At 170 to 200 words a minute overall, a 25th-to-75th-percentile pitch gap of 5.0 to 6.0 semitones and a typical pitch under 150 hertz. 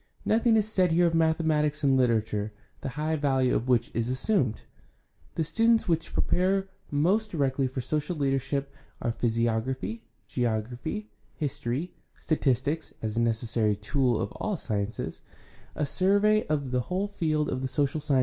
No: average, 160 wpm; wide, 5.4 semitones; medium, 140 Hz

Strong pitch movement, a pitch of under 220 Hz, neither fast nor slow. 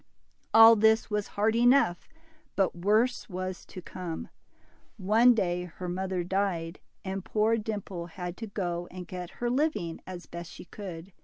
No: average, 3.7 semitones; high, 190 Hz; average, 155 wpm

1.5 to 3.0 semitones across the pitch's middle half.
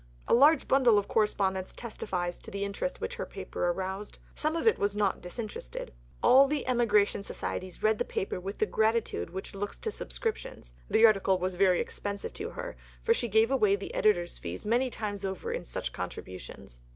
No: average, 4.1 semitones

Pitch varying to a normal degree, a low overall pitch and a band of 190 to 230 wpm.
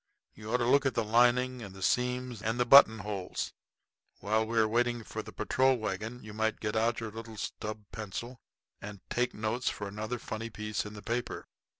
No: narrow, 2.3 semitones; low, 110 Hz; average, 200 wpm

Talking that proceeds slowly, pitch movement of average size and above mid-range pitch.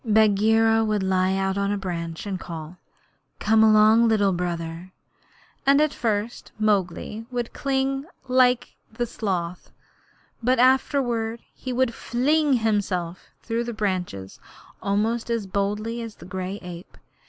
Yes: slow, 130 wpm; average, 3.9 semitones; high, 215 Hz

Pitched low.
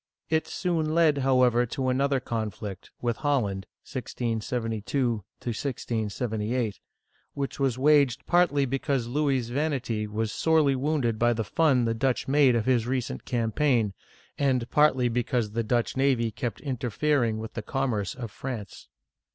Yes: low, 125 Hz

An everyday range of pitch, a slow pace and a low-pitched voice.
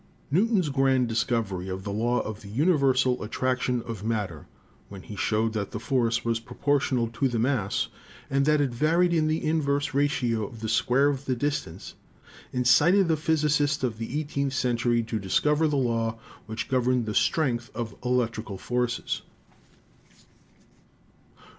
No: average, 4.0 semitones; average, 155 wpm; low, 125 Hz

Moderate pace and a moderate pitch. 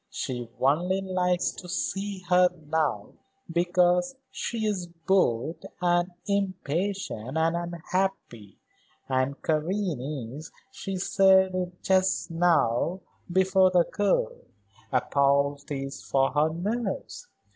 No: slow, 105 wpm; medium, 175 Hz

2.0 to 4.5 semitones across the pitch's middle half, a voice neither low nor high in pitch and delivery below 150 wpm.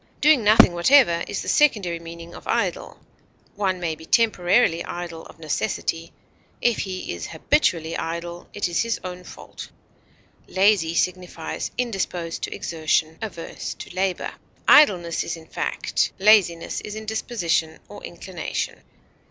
Yes: average, 4.0 semitones; medium, 175 Hz; slow, 135 wpm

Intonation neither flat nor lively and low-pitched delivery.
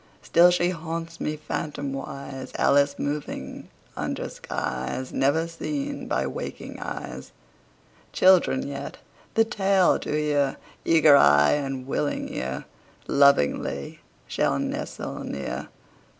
No: average, 3.7 semitones; medium, 145 Hz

